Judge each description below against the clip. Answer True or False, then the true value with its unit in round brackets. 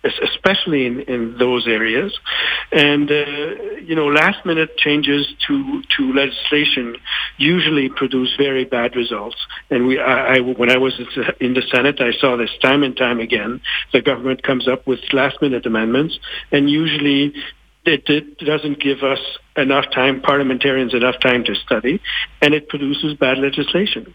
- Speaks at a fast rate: False (160 wpm)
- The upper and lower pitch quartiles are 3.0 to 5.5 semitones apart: False (2.6 semitones)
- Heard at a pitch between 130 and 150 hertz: True (140 Hz)